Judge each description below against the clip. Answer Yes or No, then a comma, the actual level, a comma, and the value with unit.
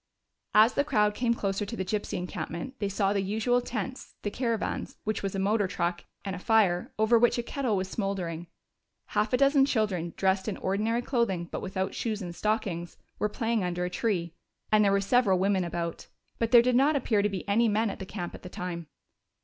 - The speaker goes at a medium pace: No, fast, 215 wpm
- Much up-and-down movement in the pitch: No, average, 3.5 semitones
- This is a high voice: Yes, high, 205 Hz